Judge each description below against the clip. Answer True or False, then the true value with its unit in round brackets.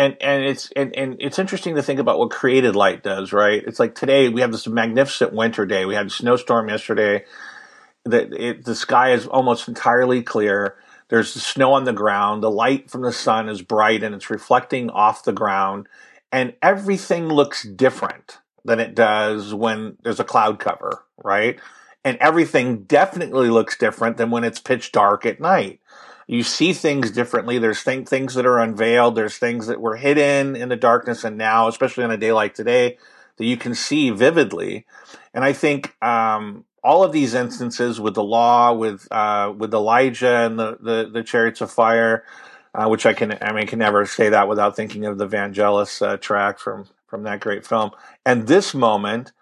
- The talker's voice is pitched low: True (115 Hz)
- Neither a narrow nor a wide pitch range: True (3.2 semitones)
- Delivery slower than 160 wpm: False (195 wpm)